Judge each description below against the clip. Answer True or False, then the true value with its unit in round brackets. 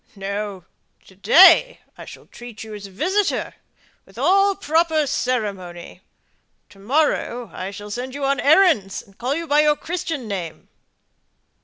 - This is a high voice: True (245 Hz)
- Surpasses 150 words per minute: False (145 wpm)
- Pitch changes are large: True (7.9 semitones)